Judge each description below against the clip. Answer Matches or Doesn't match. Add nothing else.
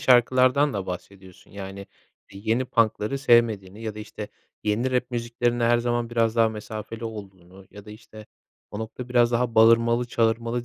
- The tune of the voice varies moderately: Doesn't match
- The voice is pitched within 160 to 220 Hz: Doesn't match